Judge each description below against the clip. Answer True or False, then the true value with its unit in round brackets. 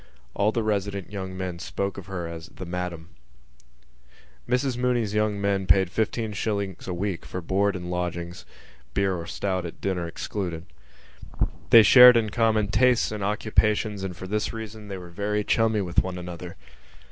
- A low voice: True (100 Hz)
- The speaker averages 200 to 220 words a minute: False (170 wpm)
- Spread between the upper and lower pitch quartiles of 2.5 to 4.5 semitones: True (3.0 semitones)